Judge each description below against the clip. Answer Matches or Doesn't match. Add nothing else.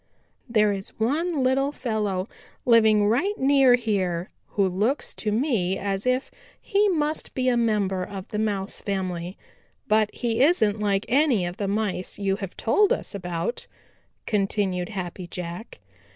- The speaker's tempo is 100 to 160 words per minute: Matches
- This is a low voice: Doesn't match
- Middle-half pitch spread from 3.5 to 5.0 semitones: Matches